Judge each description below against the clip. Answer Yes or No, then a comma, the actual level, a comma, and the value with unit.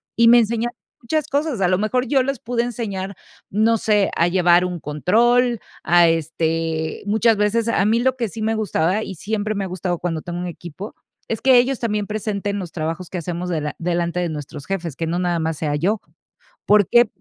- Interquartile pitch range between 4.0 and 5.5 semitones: Yes, average, 4.9 semitones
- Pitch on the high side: Yes, high, 195 Hz